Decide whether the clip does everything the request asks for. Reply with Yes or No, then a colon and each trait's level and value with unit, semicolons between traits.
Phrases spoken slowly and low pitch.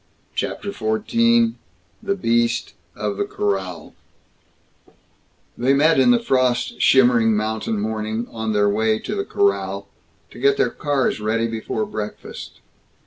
Yes: slow, 130 wpm; low, 115 Hz